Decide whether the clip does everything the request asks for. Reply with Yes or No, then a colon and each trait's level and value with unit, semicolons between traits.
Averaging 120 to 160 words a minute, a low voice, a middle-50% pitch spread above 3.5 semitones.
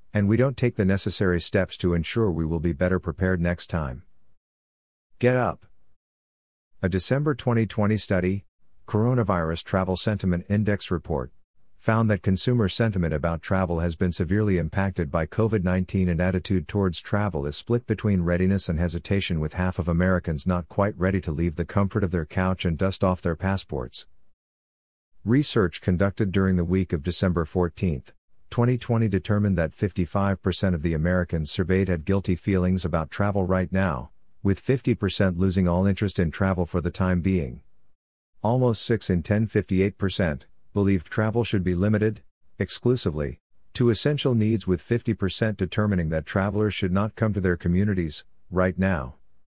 No: average, 155 wpm; very low, 95 Hz; average, 3.1 semitones